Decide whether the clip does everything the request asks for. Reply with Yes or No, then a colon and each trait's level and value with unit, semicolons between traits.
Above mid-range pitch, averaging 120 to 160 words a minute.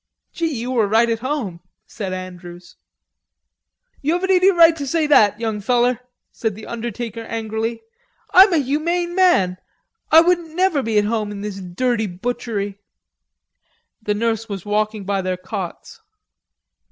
Yes: high, 225 Hz; average, 150 wpm